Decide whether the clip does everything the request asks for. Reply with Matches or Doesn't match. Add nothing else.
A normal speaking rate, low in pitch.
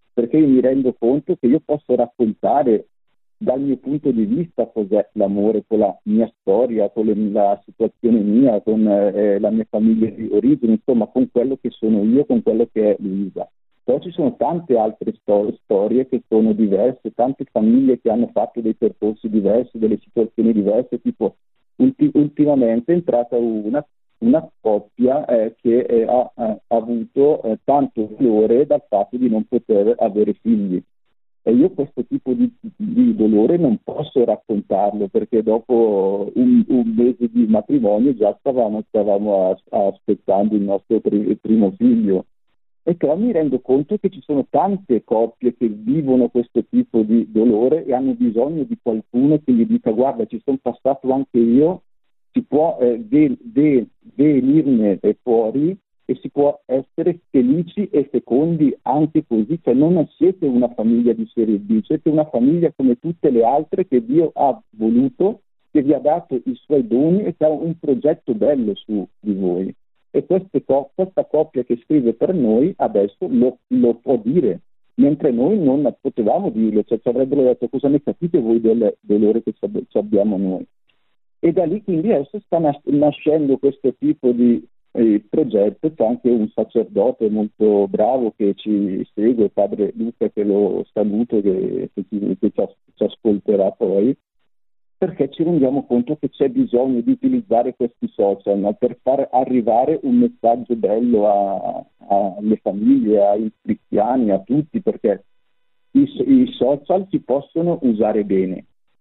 Matches